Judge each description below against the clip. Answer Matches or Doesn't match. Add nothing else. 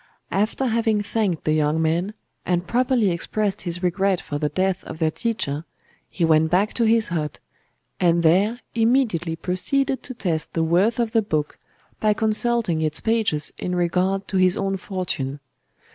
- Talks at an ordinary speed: Matches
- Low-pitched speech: Doesn't match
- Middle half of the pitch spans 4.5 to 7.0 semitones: Matches